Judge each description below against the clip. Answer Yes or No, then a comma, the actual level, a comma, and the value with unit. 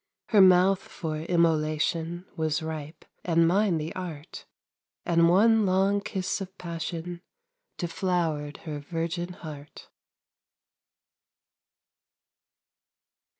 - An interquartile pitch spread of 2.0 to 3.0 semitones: Yes, narrow, 2.6 semitones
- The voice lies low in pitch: No, medium, 170 Hz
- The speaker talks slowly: Yes, slow, 90 wpm